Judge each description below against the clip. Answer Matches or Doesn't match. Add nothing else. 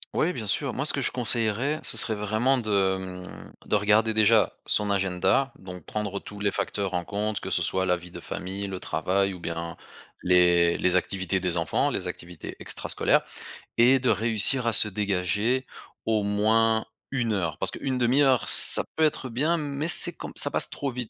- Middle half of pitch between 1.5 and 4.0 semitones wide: Doesn't match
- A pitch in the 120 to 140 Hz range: Doesn't match